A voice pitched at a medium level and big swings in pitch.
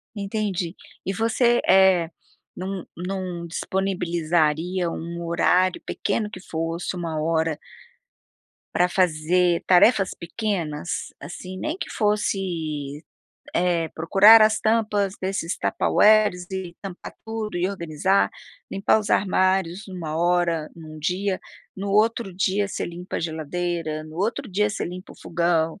No: medium, 180 Hz; average, 2.9 semitones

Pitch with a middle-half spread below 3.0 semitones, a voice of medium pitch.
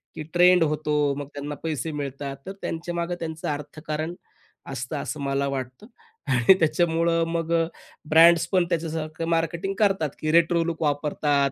Yes: narrow, 2.4 semitones; medium, 160 Hz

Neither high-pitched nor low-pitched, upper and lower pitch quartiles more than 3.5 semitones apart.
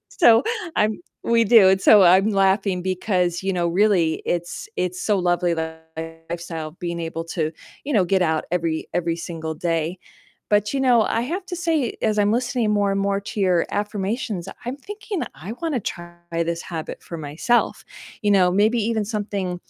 No: high, 195 Hz; average, 4.2 semitones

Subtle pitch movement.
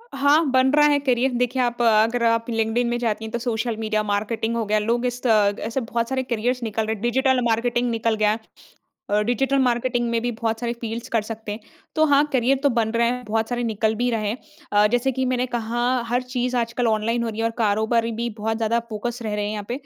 Yes: narrow, 1.9 semitones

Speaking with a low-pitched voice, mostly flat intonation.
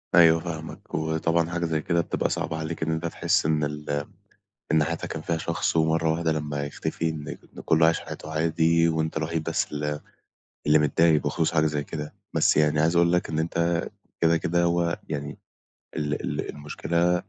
Yes: very low, 80 Hz; narrow, 1.5 semitones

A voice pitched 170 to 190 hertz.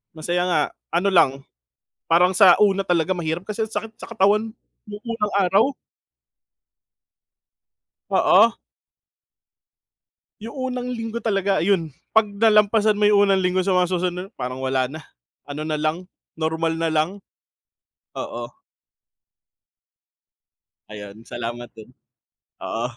Yes: medium, 185 Hz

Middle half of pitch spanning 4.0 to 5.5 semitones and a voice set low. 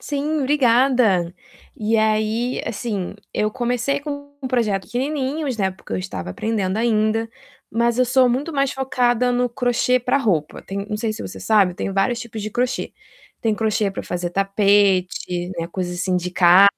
No: average, 4.3 semitones; high, 220 Hz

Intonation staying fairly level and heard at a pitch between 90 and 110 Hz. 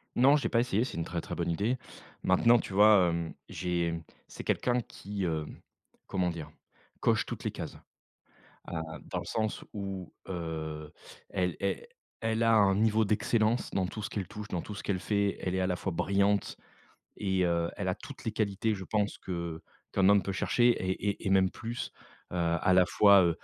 No: average, 3.3 semitones; very low, 95 Hz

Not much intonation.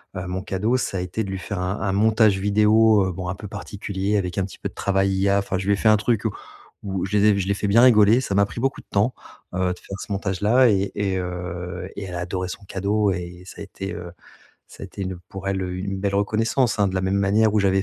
Yes: narrow, 1.9 semitones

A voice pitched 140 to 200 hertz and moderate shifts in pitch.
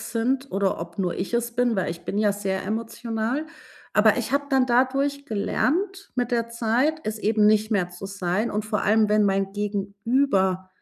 No: high, 220 Hz; average, 3.8 semitones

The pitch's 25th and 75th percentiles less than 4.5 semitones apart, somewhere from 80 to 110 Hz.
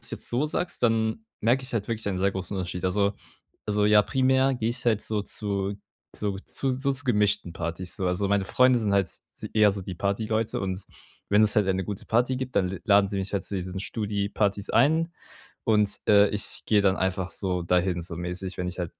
Yes: average, 2.9 semitones; low, 100 Hz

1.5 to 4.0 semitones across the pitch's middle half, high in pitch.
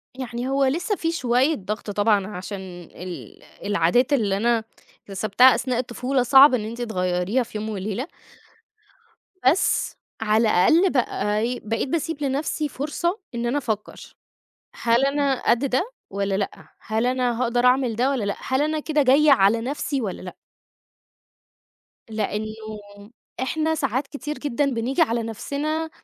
No: average, 4.6 semitones; high, 245 Hz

